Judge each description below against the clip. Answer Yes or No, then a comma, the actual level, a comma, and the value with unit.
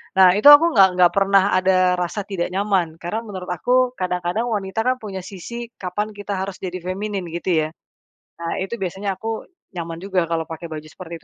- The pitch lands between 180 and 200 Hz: Yes, high, 190 Hz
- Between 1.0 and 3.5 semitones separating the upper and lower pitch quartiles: Yes, average, 2.9 semitones